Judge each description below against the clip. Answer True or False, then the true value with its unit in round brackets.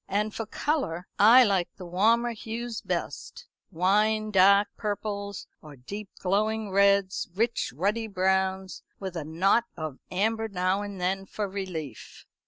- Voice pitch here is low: False (200 Hz)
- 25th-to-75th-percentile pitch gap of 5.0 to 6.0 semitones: False (2.7 semitones)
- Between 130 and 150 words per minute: True (140 wpm)